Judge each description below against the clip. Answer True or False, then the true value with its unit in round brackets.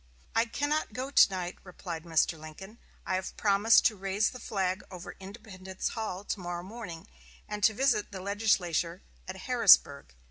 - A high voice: True (195 Hz)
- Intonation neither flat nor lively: True (3.5 semitones)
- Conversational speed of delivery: True (165 wpm)